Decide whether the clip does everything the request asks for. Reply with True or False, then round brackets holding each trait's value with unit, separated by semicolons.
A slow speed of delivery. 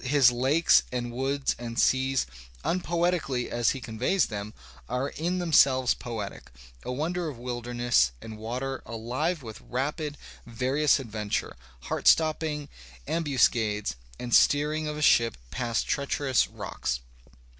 True (125 wpm)